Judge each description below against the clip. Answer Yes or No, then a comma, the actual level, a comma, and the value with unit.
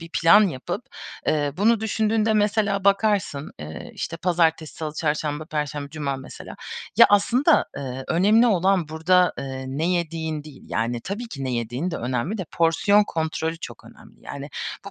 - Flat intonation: No, wide, 5.5 semitones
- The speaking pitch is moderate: Yes, medium, 165 Hz